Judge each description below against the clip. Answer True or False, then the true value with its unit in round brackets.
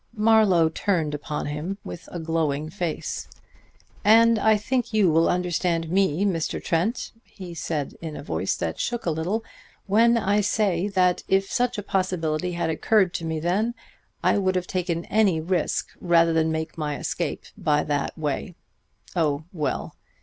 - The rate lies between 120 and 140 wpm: False (165 wpm)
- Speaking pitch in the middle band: True (175 Hz)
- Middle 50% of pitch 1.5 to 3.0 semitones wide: False (4.0 semitones)